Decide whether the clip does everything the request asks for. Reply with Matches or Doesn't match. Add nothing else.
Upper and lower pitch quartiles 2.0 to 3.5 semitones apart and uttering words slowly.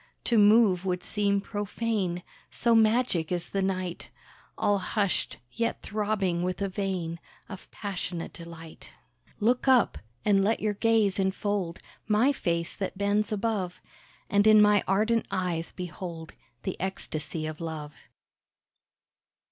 Matches